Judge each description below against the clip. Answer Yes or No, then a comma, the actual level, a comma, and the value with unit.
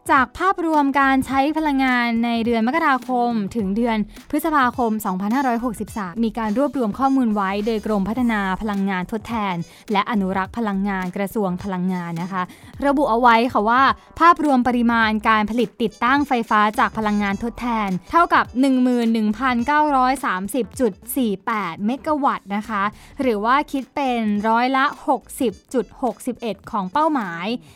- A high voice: Yes, high, 230 Hz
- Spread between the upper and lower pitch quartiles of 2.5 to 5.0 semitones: Yes, average, 4.0 semitones